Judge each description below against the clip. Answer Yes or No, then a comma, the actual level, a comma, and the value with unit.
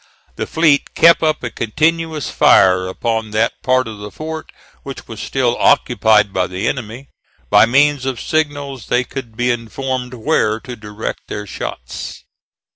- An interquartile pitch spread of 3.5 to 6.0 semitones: Yes, average, 4.5 semitones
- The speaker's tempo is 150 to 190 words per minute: Yes, average, 155 wpm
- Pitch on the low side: Yes, low, 125 Hz